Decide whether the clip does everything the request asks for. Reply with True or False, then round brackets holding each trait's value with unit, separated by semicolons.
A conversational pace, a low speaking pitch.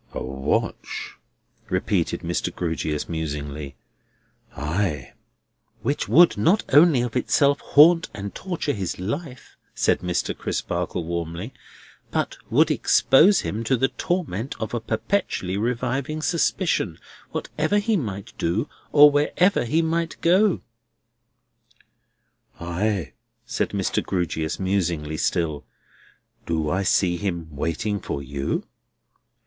False (115 wpm; 105 Hz)